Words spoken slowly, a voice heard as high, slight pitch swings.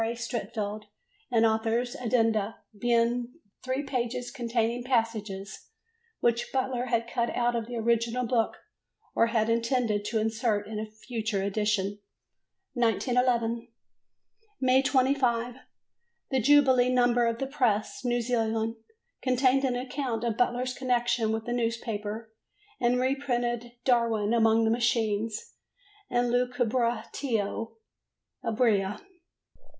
Yes: slow, 115 wpm; high, 235 Hz; narrow, 1.9 semitones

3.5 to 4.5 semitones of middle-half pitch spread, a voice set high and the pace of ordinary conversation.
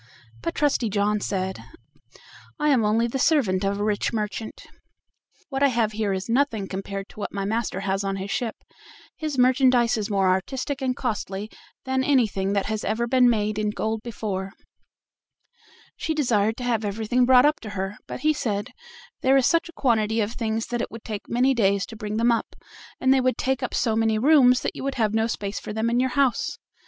No: average, 3.8 semitones; high, 225 Hz; fast, 210 wpm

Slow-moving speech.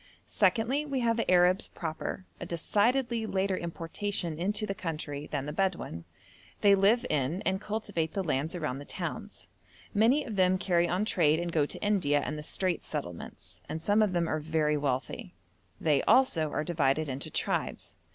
No: average, 175 wpm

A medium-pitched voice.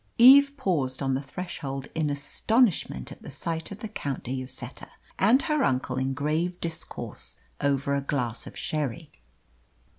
Yes: medium, 145 Hz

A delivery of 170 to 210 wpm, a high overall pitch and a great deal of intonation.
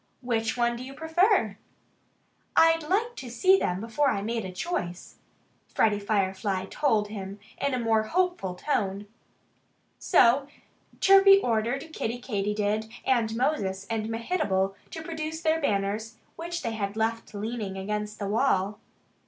No: average, 140 wpm; high, 225 Hz; wide, 6.7 semitones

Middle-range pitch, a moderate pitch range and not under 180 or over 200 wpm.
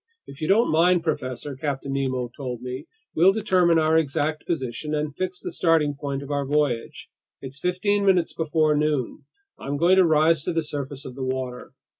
Yes: medium, 150 Hz; average, 3.5 semitones; average, 185 wpm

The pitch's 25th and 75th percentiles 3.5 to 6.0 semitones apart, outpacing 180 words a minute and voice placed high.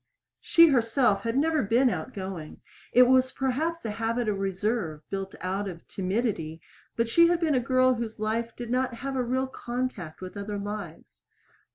No: average, 4.6 semitones; average, 175 wpm; high, 230 Hz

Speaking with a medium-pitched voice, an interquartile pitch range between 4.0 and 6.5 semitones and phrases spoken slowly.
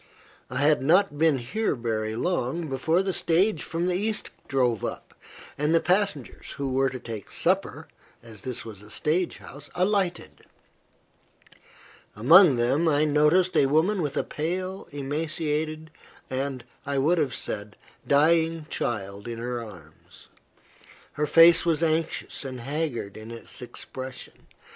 No: medium, 150 Hz; average, 5.1 semitones; average, 145 wpm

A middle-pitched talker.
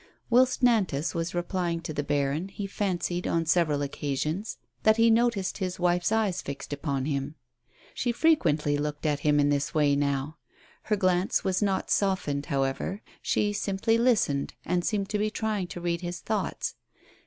Yes: medium, 175 Hz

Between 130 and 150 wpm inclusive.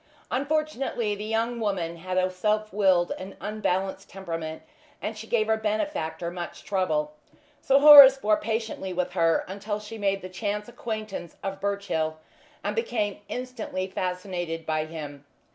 Yes: average, 145 wpm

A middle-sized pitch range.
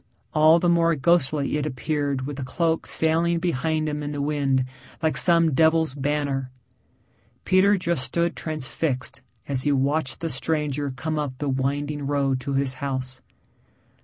Yes: average, 3.1 semitones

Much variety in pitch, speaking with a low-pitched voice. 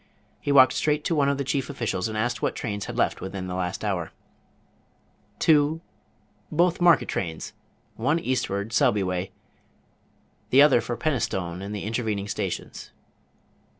Yes: wide, 6.3 semitones; low, 115 Hz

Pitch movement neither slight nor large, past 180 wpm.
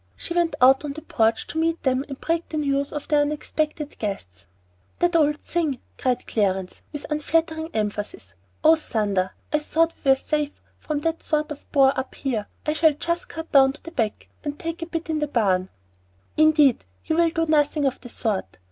Yes: average, 3.8 semitones; average, 200 wpm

